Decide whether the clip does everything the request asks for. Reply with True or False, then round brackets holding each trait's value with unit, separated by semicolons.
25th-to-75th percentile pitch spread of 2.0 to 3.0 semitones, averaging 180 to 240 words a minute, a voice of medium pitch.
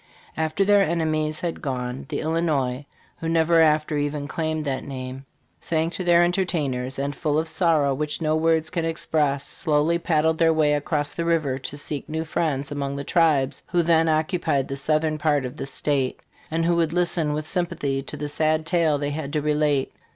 True (2.4 semitones; 190 wpm; 155 Hz)